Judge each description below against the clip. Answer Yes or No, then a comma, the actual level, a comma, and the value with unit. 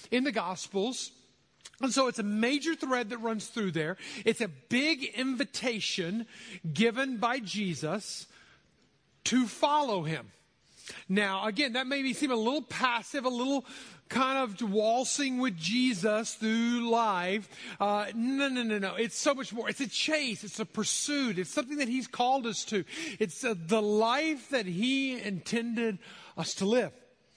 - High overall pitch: Yes, high, 230 Hz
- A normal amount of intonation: Yes, average, 3.9 semitones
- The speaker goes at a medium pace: Yes, average, 160 wpm